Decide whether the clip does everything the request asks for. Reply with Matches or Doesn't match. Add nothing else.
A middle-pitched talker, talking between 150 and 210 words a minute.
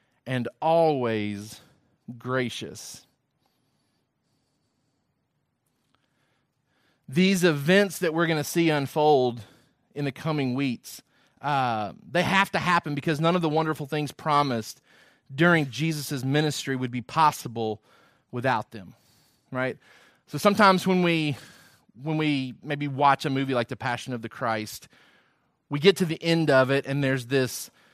Doesn't match